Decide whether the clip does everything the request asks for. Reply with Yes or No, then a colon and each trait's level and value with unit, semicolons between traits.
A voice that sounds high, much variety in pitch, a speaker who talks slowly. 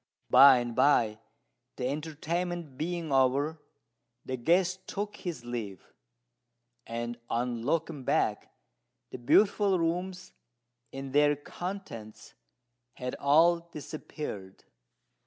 No: medium, 145 Hz; wide, 5.7 semitones; slow, 100 wpm